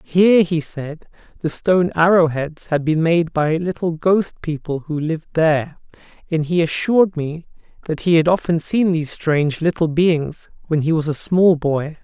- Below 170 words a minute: No, average, 180 wpm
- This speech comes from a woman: No, male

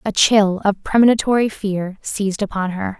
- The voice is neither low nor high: No, high, 200 Hz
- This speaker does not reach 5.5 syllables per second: Yes, 5.0 syllables/s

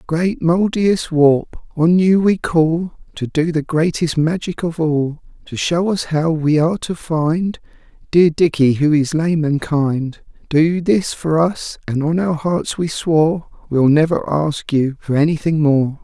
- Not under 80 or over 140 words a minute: No, average, 170 wpm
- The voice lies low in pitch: No, medium, 160 Hz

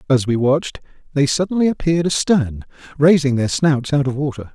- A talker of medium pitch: Yes, medium, 145 Hz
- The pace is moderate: Yes, average, 170 wpm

